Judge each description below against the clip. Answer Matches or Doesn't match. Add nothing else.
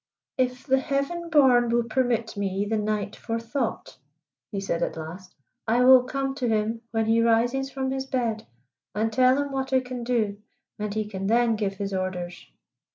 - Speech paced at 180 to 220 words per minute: Matches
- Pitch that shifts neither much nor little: Matches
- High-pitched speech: Matches